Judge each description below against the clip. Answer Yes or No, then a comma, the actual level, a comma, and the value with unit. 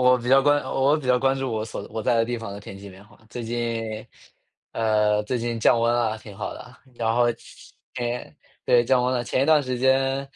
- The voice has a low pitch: Yes, low, 120 Hz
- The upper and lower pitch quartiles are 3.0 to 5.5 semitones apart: No, narrow, 2.6 semitones